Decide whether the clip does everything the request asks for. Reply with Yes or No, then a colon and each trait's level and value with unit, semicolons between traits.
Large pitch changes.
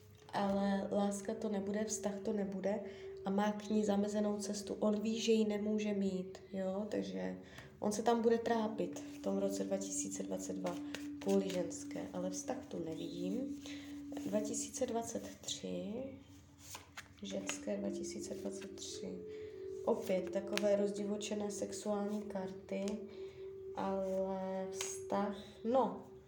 Yes: wide, 7.2 semitones